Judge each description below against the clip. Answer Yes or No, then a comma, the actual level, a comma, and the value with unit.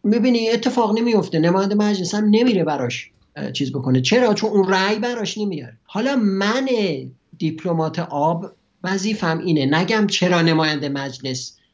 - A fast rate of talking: No, average, 135 wpm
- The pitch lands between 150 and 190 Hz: Yes, medium, 185 Hz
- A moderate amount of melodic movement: No, wide, 6.0 semitones